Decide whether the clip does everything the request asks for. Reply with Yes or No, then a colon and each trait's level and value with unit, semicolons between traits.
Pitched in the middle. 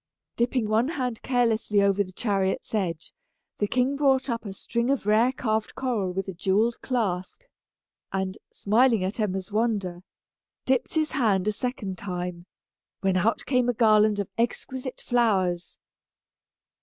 No: high, 215 Hz